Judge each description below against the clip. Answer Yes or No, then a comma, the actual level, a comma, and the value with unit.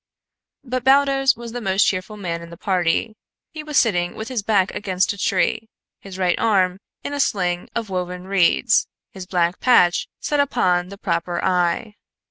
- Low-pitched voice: No, high, 195 Hz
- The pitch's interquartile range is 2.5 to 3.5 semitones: No, average, 4.2 semitones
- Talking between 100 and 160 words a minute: No, average, 175 wpm